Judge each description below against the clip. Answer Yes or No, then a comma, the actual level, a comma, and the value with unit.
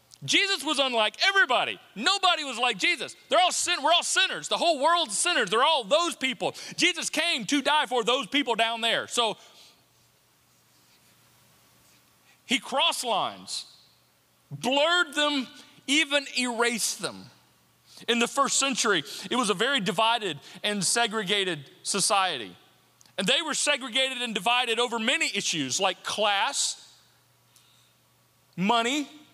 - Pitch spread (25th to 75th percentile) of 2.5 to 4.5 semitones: No, average, 5.3 semitones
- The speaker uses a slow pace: Yes, slow, 130 wpm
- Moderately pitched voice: No, very high, 265 Hz